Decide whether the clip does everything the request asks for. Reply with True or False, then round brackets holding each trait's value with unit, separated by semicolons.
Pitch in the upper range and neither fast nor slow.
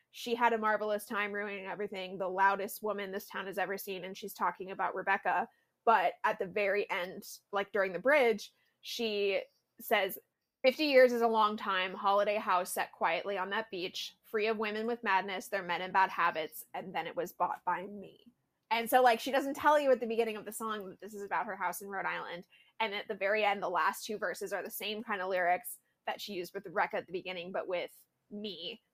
False (200 Hz; 225 wpm)